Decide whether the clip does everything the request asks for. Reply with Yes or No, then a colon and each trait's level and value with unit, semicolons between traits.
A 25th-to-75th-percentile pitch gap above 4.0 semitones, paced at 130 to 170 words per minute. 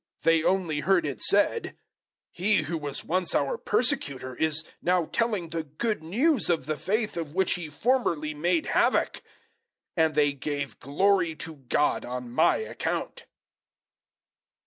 Yes: average, 4.7 semitones; average, 150 wpm